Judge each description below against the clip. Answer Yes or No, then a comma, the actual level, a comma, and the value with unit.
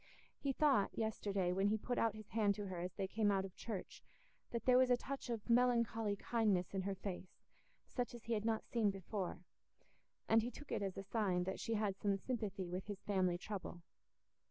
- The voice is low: No, high, 205 Hz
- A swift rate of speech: Yes, fast, 210 wpm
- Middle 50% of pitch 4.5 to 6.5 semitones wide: No, average, 3.1 semitones